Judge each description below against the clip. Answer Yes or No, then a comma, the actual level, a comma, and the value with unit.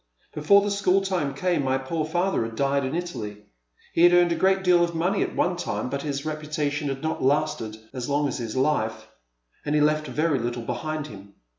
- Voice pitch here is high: No, medium, 150 Hz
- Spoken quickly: Yes, fast, 210 wpm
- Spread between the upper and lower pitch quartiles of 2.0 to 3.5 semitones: No, average, 4.5 semitones